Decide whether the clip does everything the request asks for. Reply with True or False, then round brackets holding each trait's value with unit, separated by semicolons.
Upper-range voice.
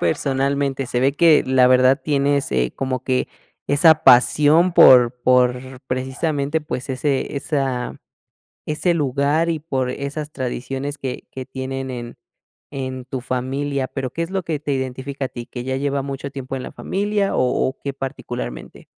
False (135 Hz)